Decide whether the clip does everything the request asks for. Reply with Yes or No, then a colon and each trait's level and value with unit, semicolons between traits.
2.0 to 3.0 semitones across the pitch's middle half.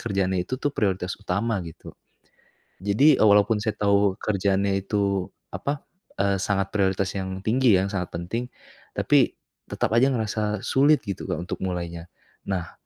Yes: narrow, 2.4 semitones